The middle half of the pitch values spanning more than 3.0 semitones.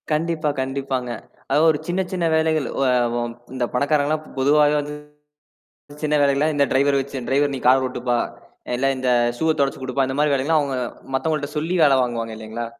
No: narrow, 2.6 semitones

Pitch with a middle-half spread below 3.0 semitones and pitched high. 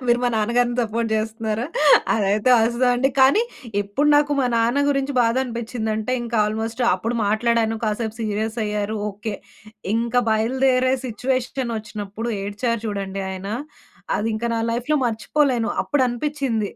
Yes: narrow, 2.5 semitones; high, 230 Hz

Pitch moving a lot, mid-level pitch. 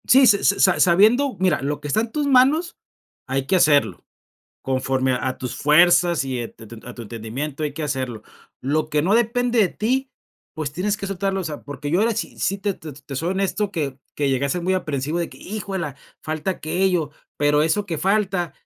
Yes: wide, 5.9 semitones; medium, 165 Hz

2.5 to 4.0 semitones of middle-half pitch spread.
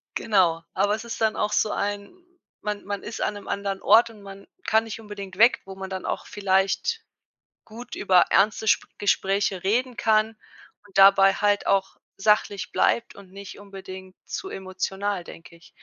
No: narrow, 1.9 semitones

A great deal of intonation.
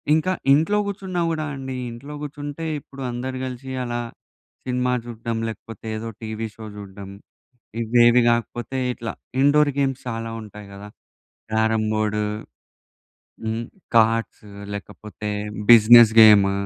No: average, 3.4 semitones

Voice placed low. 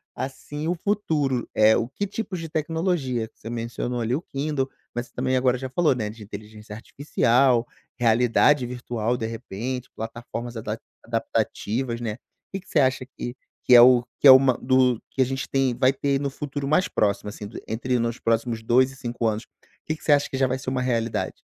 Yes: low, 125 Hz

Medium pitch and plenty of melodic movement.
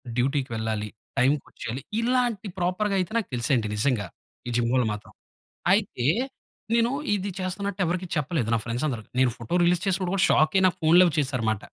Yes: medium, 150 Hz; wide, 7.5 semitones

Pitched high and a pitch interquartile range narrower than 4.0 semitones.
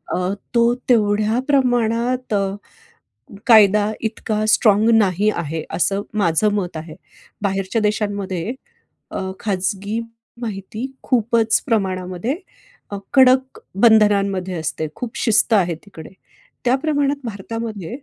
Yes: high, 210 Hz; average, 3.3 semitones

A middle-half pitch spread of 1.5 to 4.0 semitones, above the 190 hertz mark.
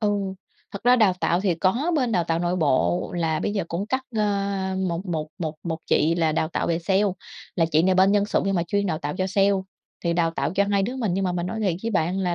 No: average, 3.3 semitones; medium, 185 Hz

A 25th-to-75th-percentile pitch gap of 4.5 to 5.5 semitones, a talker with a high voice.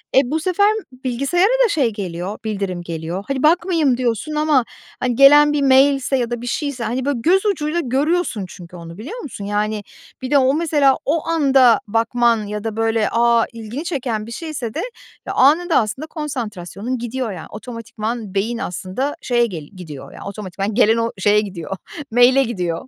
Yes: average, 5.2 semitones; high, 240 Hz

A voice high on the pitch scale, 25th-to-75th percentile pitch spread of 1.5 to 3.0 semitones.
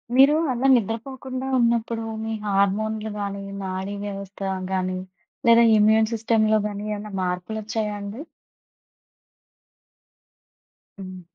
Yes: high, 215 Hz; narrow, 2.4 semitones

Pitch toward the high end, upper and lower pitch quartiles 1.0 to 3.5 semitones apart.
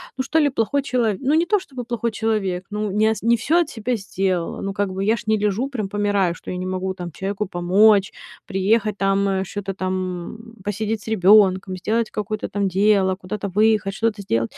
Yes: high, 205 Hz; average, 2.8 semitones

